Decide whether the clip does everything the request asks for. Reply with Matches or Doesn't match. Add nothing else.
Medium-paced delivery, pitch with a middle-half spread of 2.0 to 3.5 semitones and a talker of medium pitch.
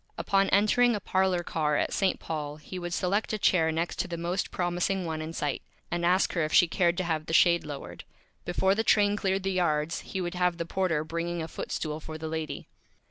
Doesn't match